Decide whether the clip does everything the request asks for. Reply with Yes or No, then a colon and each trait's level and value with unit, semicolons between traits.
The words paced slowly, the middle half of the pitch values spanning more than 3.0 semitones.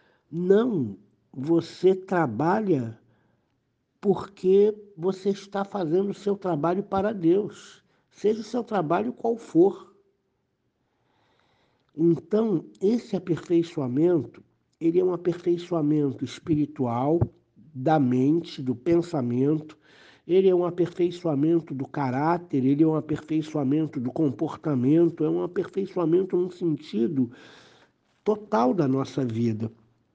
Yes: slow, 100 wpm; average, 5.3 semitones